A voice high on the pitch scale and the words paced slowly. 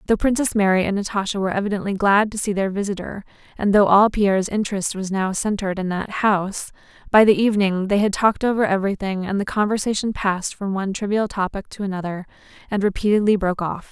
No: high, 200 Hz; average, 195 wpm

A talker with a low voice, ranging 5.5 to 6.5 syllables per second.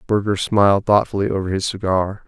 Yes: low, 100 Hz; 5.6 syllables/s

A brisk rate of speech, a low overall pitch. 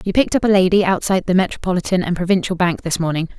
No: fast, 230 wpm; medium, 185 Hz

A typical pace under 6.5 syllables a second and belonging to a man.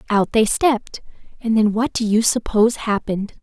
No: 5.4 syllables/s; female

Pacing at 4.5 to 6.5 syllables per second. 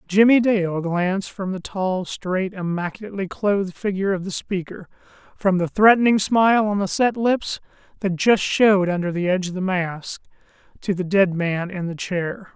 Yes: 5.0 syllables/s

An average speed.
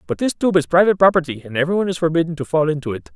No: fast, 265 wpm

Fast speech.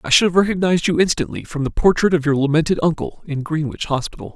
Yes: fast, 220 wpm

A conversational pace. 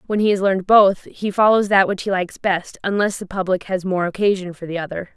No: fast, 245 wpm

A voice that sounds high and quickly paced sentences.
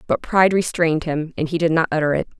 No: medium, 160 Hz; fast, 250 wpm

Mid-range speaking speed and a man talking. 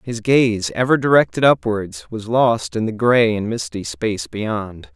Yes: average, 170 wpm; male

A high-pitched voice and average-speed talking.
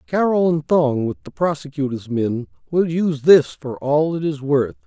No: medium, 150 Hz; average, 185 wpm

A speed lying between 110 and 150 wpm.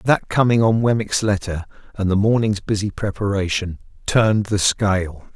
Yes: average, 145 wpm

